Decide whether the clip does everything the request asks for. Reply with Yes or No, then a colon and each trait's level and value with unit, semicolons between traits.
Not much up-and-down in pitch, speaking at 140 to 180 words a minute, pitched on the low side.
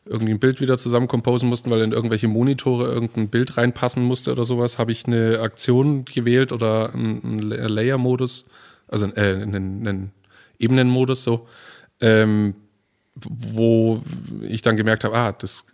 Yes: narrow, 2.3 semitones; average, 150 wpm; low, 115 Hz